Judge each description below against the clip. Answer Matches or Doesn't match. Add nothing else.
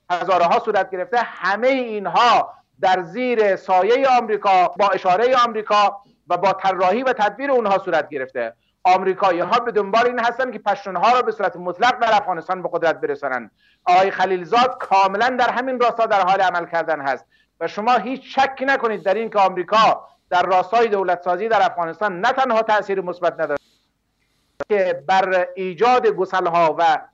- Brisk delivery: Matches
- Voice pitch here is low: Doesn't match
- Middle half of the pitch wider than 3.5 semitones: Matches